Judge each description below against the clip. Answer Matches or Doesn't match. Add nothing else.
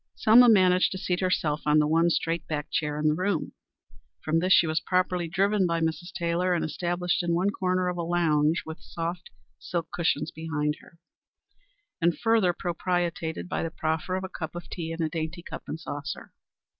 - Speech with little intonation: Matches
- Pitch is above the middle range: Doesn't match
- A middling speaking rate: Matches